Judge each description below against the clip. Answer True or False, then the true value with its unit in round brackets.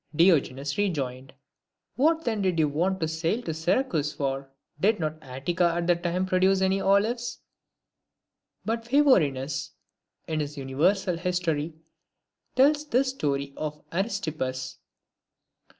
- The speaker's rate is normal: False (130 wpm)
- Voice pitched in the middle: True (170 Hz)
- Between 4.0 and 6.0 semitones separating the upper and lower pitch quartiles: True (5.2 semitones)